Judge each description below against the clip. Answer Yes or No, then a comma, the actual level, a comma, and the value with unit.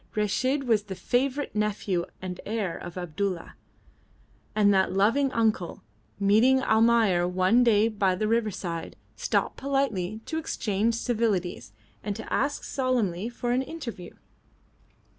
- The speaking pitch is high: Yes, high, 215 Hz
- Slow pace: Yes, slow, 125 wpm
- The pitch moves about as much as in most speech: Yes, average, 4.3 semitones